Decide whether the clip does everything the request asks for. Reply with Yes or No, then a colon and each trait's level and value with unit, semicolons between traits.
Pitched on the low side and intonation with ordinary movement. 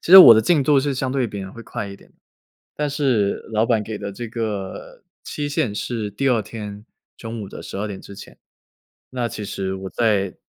Yes: low, 110 Hz; average, 4.0 semitones